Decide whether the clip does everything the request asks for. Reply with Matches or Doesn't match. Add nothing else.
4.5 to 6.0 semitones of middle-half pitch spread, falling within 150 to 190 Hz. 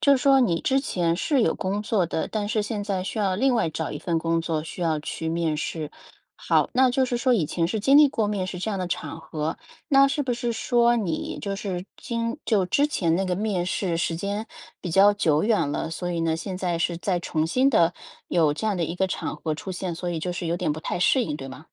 Matches